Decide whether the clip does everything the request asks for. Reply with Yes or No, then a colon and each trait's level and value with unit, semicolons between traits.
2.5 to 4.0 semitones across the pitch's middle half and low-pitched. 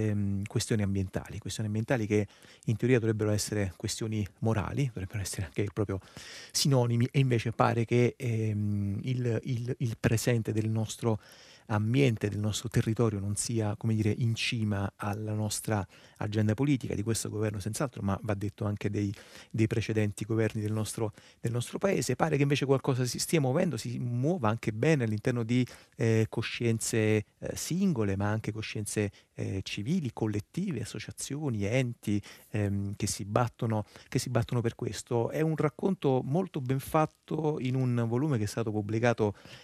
Yes: average, 3.2 semitones; low, 115 Hz